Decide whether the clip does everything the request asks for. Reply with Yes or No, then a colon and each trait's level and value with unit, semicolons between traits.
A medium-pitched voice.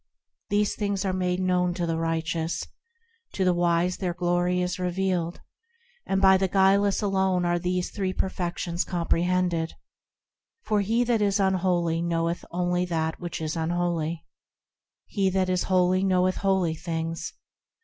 Yes: medium, 180 Hz